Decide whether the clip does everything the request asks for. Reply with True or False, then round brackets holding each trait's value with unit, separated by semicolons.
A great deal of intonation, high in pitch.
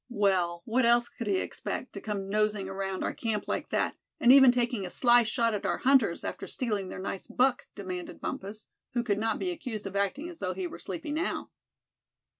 False (3.9 semitones; 215 Hz)